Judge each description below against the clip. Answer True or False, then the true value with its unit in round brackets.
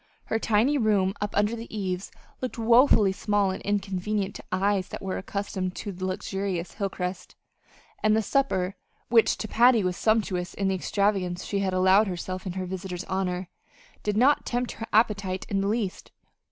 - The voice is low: False (195 Hz)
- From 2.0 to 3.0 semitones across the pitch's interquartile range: True (2.5 semitones)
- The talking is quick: False (170 wpm)